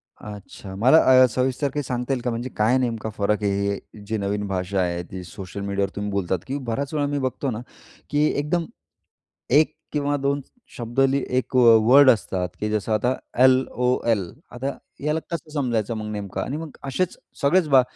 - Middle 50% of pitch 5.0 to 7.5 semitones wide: Yes, wide, 5.4 semitones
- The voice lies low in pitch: Yes, low, 120 Hz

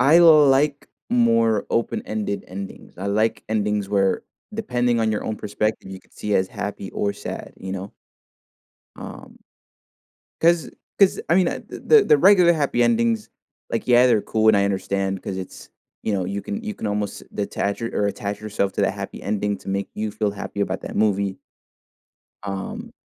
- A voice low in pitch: Yes, low, 105 Hz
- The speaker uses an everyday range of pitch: Yes, average, 3.5 semitones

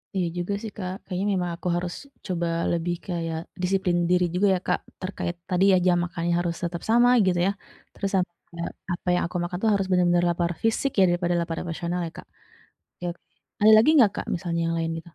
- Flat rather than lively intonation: Yes, narrow, 1.6 semitones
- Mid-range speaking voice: Yes, medium, 180 Hz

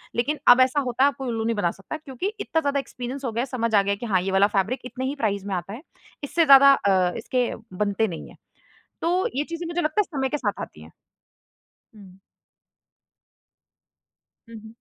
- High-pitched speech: Yes, high, 245 Hz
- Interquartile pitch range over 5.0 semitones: Yes, wide, 5.6 semitones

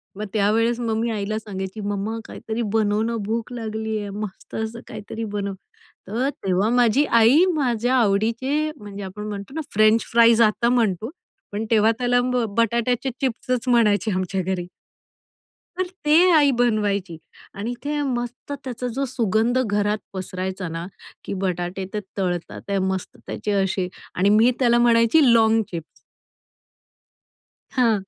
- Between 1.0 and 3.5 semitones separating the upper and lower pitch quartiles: Yes, average, 3.0 semitones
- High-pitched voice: Yes, high, 220 Hz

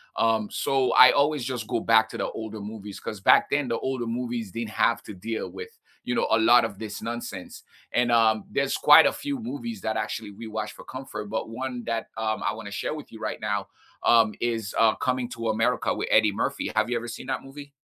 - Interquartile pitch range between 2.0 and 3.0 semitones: Yes, average, 2.7 semitones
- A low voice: Yes, low, 115 Hz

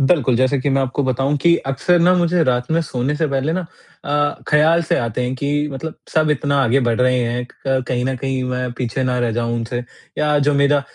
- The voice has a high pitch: No, low, 135 Hz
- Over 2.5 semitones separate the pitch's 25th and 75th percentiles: Yes, average, 2.9 semitones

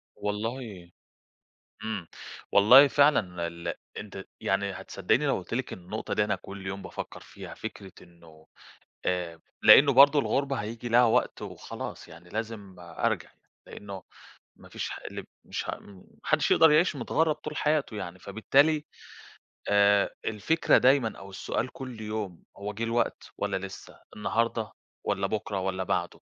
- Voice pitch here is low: Yes, low, 105 Hz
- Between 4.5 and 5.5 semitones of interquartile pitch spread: Yes, average, 5.1 semitones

